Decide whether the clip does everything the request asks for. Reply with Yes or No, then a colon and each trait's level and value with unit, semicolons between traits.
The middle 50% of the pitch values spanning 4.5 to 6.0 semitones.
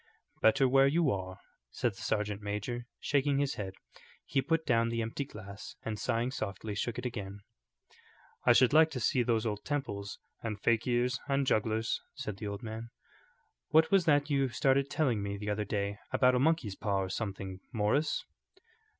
Yes: average, 4.8 semitones